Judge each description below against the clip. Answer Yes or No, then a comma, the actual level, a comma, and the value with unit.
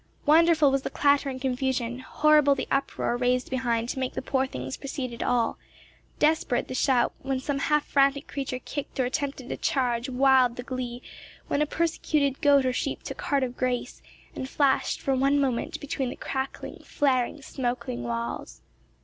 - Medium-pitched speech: No, very high, 265 Hz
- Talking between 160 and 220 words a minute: Yes, average, 175 wpm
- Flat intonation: Yes, narrow, 2.1 semitones